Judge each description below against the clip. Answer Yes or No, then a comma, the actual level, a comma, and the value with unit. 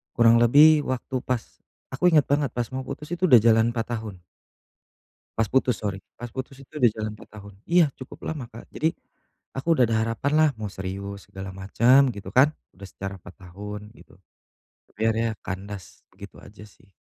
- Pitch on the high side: No, low, 115 Hz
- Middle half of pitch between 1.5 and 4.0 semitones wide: No, average, 4.5 semitones